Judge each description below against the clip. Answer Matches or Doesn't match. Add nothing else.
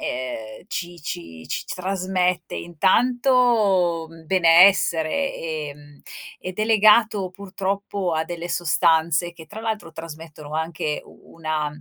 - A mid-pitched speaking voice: Matches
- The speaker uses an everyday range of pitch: Matches